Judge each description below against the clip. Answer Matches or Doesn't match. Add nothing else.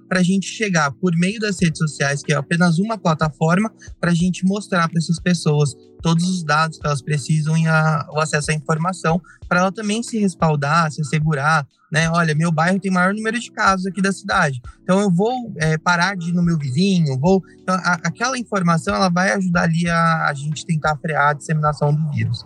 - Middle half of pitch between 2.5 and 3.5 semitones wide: Matches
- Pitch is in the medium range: Matches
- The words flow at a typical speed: Doesn't match